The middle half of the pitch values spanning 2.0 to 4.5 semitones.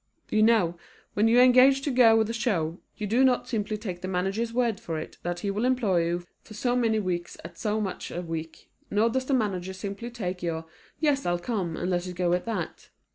No: average, 4.9 semitones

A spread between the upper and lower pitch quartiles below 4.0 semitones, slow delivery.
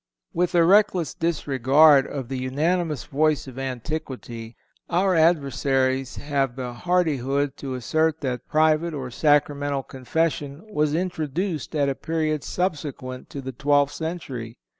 Yes: average, 3.4 semitones; slow, 130 wpm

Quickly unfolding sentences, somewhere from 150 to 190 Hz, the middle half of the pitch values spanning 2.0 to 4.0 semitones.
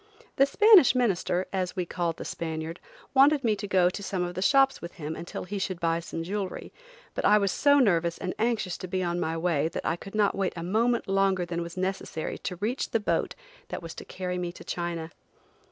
Yes: fast, 225 wpm; medium, 185 Hz; average, 3.4 semitones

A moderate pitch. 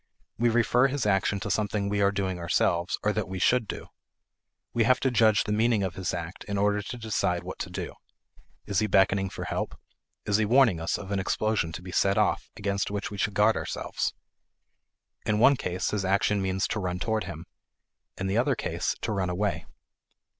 No: low, 100 Hz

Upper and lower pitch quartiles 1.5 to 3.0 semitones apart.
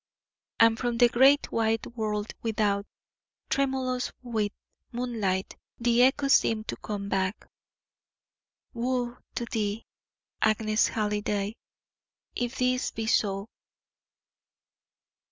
Yes: average, 2.7 semitones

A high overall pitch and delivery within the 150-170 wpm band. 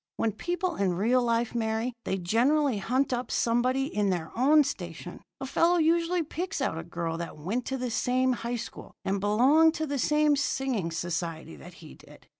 No: high, 240 Hz; average, 190 wpm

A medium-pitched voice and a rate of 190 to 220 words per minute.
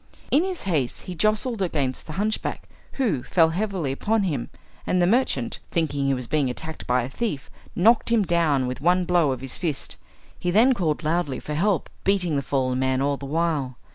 Yes: medium, 160 Hz; average, 200 wpm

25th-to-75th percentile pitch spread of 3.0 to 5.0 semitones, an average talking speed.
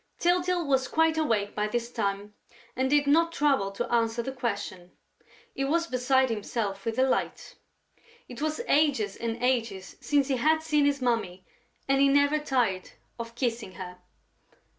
Yes: average, 4.7 semitones; average, 160 wpm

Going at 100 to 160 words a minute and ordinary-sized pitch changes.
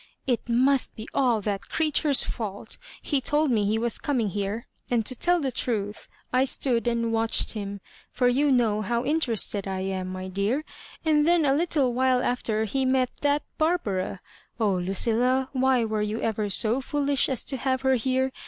No: average, 190 wpm; average, 4.0 semitones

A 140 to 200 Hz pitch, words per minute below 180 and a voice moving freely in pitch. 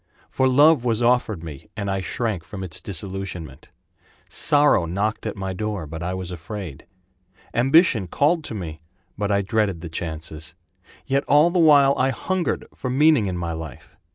No: low, 100 Hz; average, 170 wpm; wide, 7.3 semitones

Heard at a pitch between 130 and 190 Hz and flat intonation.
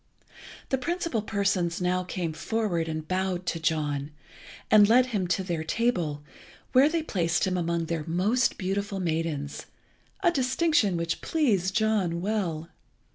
No: medium, 185 Hz; average, 4.7 semitones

